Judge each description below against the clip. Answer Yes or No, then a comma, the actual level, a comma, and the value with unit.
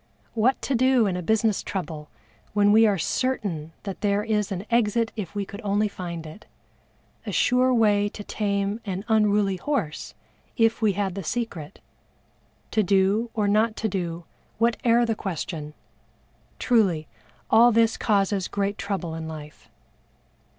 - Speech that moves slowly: No, average, 150 wpm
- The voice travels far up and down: No, average, 3.1 semitones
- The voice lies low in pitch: No, high, 205 Hz